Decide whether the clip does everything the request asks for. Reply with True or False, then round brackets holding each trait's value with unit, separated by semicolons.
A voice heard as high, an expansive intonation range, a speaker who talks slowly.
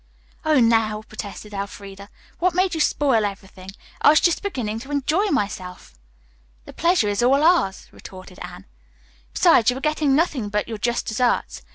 False (235 Hz; 6.9 semitones; 165 wpm)